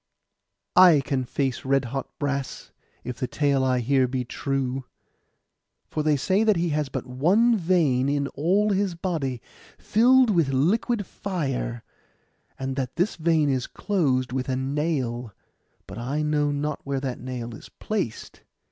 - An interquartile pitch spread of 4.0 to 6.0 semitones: Yes, average, 4.7 semitones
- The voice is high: No, medium, 140 Hz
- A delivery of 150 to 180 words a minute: Yes, average, 155 wpm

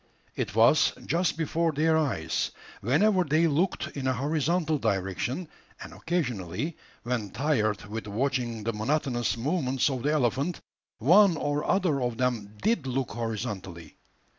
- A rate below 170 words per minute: Yes, average, 140 wpm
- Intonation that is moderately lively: No, wide, 5.8 semitones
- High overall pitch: No, low, 135 Hz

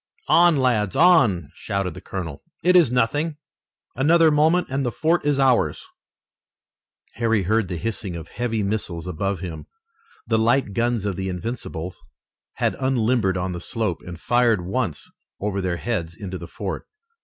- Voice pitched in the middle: No, low, 110 Hz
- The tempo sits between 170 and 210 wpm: No, average, 155 wpm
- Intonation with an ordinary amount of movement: No, wide, 5.8 semitones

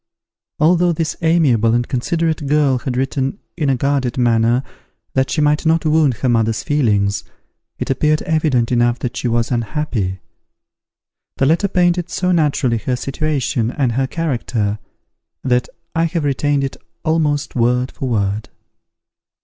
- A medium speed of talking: Yes, average, 145 wpm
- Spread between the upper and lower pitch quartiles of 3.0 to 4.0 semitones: No, average, 4.5 semitones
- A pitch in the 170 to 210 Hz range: No, low, 135 Hz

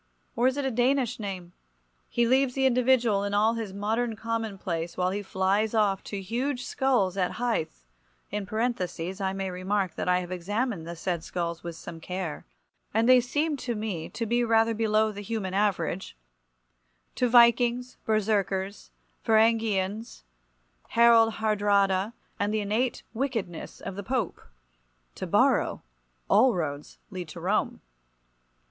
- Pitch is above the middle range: Yes, high, 210 Hz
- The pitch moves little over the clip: No, average, 3.8 semitones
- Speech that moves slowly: No, average, 150 wpm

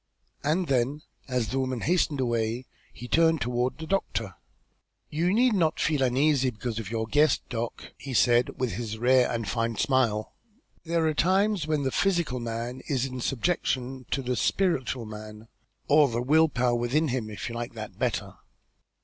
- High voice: No, low, 130 Hz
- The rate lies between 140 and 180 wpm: Yes, average, 175 wpm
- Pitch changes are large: No, average, 4.5 semitones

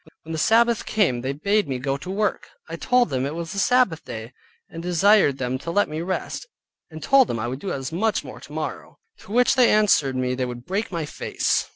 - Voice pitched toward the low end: No, medium, 165 Hz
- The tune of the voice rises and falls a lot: Yes, wide, 7.8 semitones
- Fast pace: Yes, fast, 230 wpm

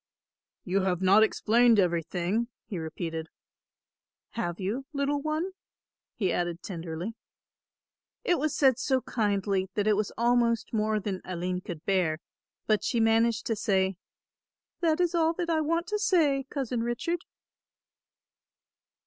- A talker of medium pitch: No, high, 220 Hz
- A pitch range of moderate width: No, wide, 6.6 semitones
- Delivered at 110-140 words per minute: Yes, slow, 135 wpm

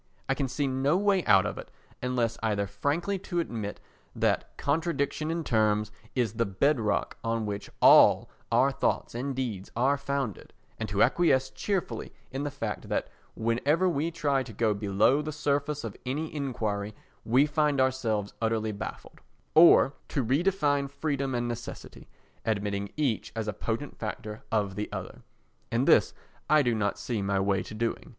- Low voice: Yes, low, 125 Hz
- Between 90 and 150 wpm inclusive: No, average, 165 wpm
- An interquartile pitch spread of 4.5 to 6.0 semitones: Yes, average, 5.1 semitones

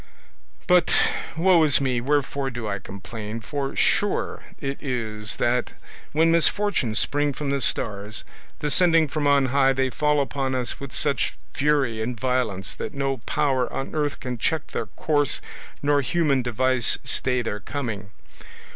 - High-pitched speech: No, low, 135 Hz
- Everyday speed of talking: Yes, average, 150 wpm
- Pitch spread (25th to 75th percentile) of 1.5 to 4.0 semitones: Yes, average, 3.4 semitones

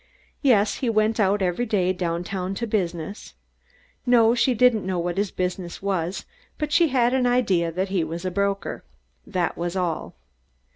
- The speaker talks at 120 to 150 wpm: No, average, 165 wpm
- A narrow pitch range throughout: No, average, 4.4 semitones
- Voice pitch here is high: Yes, high, 195 Hz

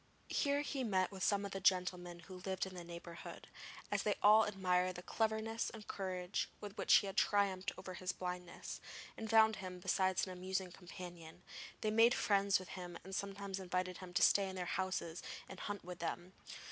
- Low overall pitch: No, high, 190 Hz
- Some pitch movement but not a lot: No, narrow, 2.0 semitones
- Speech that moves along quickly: No, average, 195 wpm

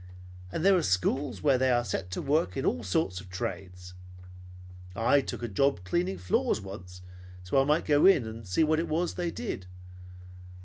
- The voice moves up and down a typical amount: No, wide, 8.1 semitones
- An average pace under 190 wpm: No, average, 195 wpm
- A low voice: Yes, low, 115 Hz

